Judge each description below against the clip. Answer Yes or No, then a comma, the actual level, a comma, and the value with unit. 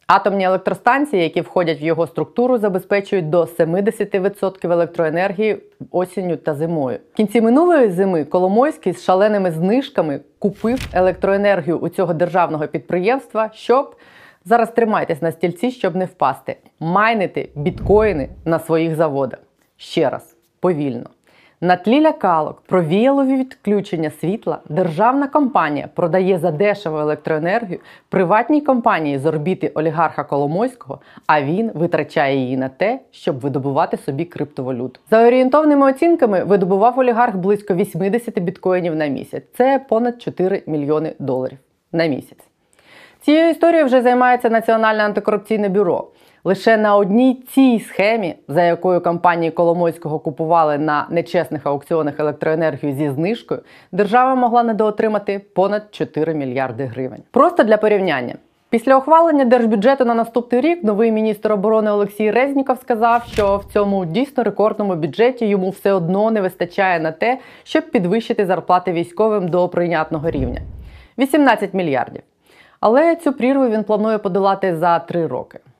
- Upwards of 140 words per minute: No, average, 130 wpm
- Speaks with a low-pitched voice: No, high, 195 Hz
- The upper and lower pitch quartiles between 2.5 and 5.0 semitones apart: No, wide, 5.6 semitones